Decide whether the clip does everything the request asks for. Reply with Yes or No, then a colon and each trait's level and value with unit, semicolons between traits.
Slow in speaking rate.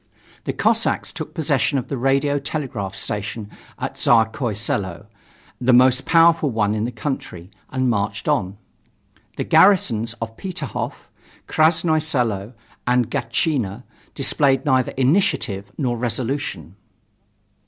Yes: slow, 120 wpm